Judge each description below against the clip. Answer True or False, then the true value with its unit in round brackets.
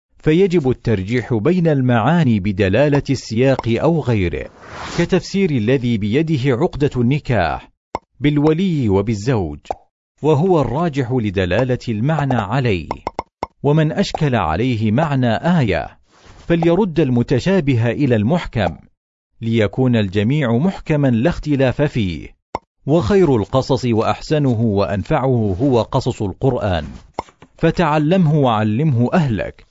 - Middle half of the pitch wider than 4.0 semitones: True (5.2 semitones)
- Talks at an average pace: True (90 wpm)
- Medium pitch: False (130 Hz)